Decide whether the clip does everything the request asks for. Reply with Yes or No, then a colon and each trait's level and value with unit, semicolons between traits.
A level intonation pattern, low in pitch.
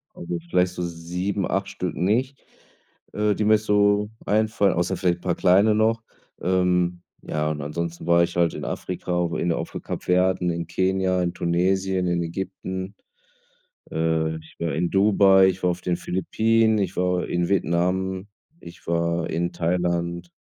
Yes: narrow, 2.1 semitones; very low, 90 Hz